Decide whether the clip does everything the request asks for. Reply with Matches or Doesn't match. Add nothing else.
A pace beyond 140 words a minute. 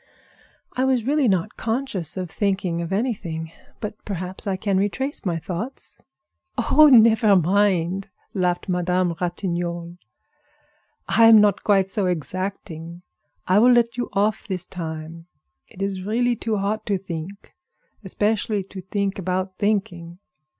Doesn't match